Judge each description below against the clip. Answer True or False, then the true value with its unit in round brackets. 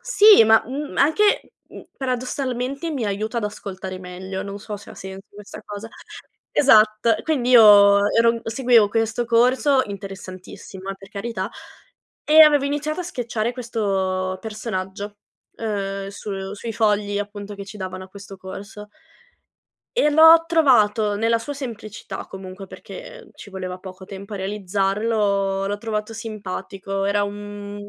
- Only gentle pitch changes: False (3.3 semitones)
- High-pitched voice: True (210 Hz)